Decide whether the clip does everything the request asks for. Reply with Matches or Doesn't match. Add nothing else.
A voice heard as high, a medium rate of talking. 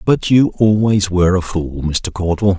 Doesn't match